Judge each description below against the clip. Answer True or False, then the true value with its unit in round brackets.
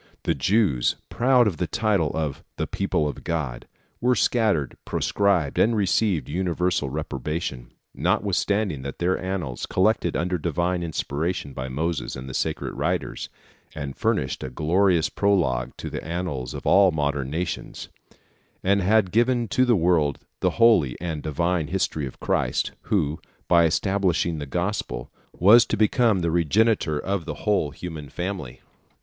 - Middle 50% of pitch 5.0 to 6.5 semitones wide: True (5.3 semitones)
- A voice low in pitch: True (85 Hz)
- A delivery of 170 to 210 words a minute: False (155 wpm)